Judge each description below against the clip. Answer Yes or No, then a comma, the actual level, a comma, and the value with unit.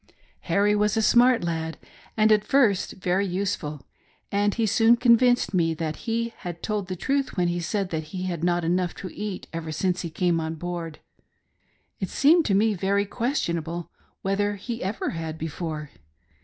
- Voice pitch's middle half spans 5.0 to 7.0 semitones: No, average, 4.1 semitones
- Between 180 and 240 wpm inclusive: Yes, average, 185 wpm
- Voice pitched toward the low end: No, high, 190 Hz